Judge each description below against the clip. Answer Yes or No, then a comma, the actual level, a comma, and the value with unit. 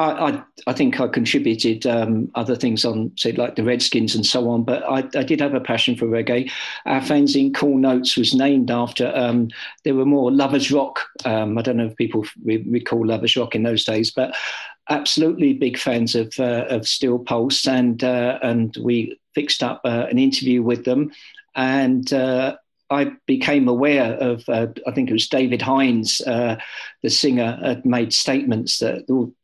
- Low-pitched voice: Yes, low, 125 Hz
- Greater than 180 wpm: Yes, average, 190 wpm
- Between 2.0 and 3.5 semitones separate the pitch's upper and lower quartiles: Yes, narrow, 2.4 semitones